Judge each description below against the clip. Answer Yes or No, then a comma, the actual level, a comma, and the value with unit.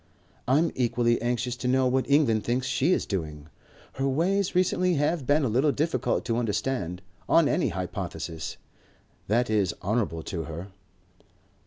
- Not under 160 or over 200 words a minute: No, average, 150 wpm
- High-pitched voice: No, low, 120 Hz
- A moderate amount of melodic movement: No, wide, 6.3 semitones